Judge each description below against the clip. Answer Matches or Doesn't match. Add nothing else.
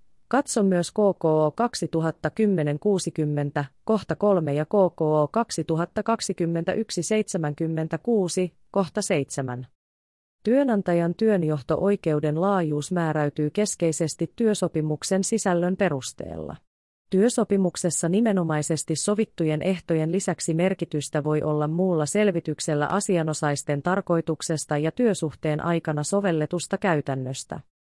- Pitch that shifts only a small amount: Doesn't match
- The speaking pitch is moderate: Matches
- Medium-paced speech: Doesn't match